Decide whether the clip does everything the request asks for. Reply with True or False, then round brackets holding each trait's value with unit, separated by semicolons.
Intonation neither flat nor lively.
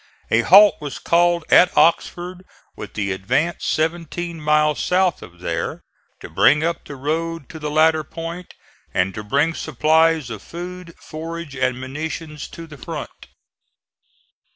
True (3.1 semitones)